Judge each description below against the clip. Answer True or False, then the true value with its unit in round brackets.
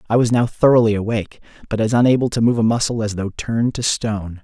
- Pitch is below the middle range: True (110 Hz)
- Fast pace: True (230 wpm)